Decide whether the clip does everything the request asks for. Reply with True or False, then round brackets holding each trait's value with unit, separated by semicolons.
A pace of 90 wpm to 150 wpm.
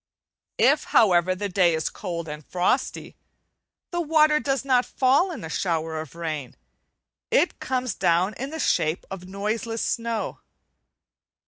True (140 wpm)